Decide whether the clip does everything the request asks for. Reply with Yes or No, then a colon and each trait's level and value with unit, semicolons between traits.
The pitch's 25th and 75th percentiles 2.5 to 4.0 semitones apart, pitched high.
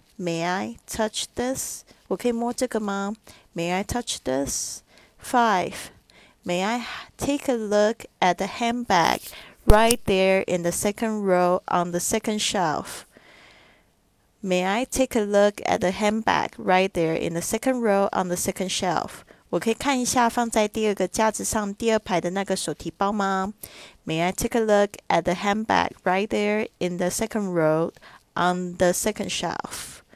Yes: average, 3.7 semitones; high, 195 Hz